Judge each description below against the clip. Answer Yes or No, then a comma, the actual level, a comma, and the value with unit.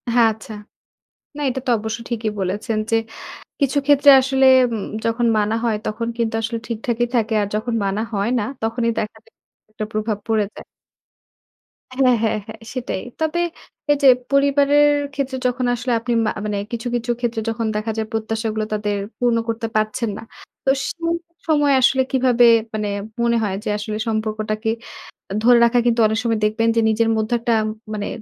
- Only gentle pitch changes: Yes, narrow, 2.3 semitones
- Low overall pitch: No, high, 230 Hz